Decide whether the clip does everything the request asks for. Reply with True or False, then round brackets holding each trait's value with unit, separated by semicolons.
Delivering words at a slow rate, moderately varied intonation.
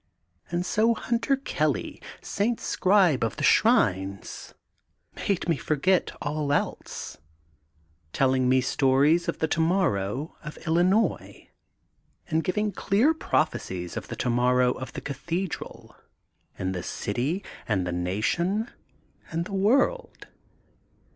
False (120 wpm; 7.5 semitones)